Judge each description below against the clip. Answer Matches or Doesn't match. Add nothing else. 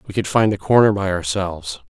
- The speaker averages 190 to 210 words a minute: Doesn't match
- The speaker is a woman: Doesn't match